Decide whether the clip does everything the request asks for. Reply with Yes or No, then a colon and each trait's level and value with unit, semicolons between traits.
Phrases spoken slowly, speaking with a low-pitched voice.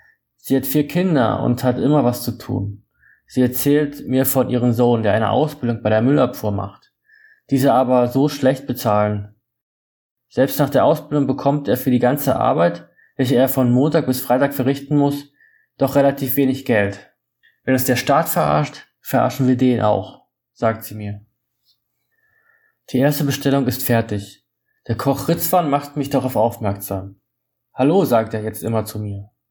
No: average, 165 wpm; low, 130 Hz